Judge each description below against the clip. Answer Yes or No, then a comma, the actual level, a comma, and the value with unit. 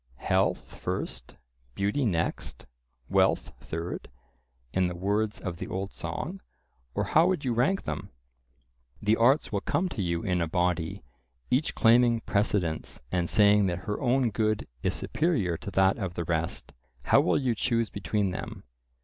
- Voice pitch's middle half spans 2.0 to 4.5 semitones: No, average, 5.1 semitones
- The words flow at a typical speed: Yes, average, 155 wpm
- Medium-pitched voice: No, low, 100 Hz